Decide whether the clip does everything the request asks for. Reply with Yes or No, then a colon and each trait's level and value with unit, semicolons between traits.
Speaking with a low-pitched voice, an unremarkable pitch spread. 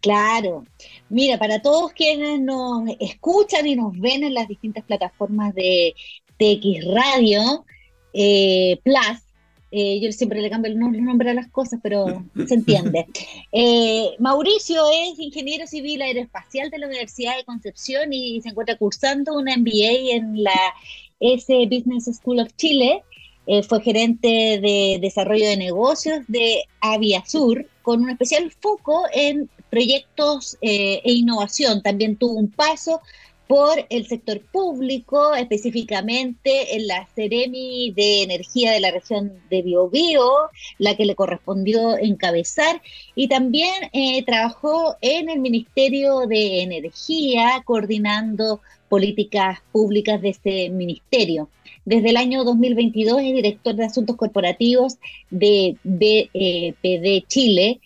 No: high, 230 Hz; average, 4.5 semitones